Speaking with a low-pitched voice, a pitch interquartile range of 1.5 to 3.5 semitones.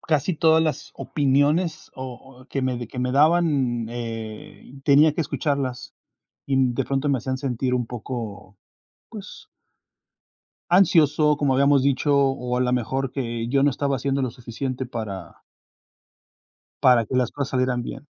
Yes: low, 130 Hz; narrow, 2.6 semitones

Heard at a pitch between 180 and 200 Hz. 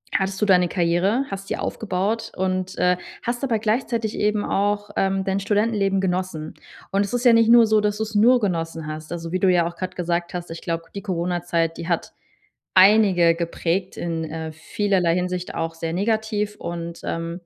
Yes: medium, 185 Hz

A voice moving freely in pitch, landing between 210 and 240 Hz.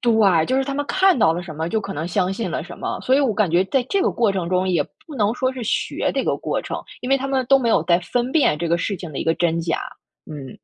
No: wide, 7.2 semitones; high, 200 Hz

